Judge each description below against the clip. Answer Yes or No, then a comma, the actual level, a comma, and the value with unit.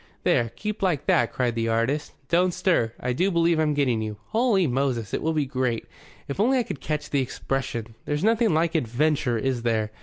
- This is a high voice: No, medium, 140 Hz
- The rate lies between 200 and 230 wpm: Yes, fast, 205 wpm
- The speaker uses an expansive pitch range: Yes, wide, 6.1 semitones